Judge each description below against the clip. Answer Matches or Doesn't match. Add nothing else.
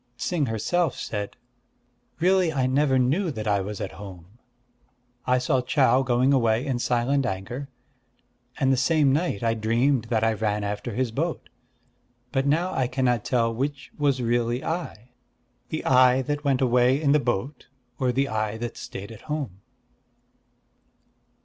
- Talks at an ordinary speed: Matches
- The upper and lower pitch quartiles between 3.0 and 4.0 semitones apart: Matches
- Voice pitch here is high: Doesn't match